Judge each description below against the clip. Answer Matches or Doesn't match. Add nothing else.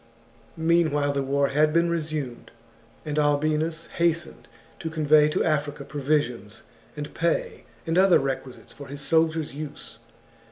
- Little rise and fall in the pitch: Matches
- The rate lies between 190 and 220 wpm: Doesn't match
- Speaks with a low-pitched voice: Doesn't match